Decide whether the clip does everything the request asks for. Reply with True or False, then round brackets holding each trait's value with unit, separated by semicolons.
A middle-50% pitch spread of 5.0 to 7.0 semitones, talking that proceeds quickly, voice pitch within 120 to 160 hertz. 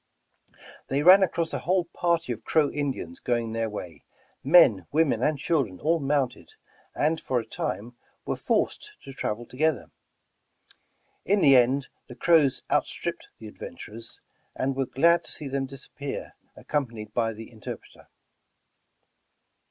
False (5.4 semitones; 160 wpm; 135 Hz)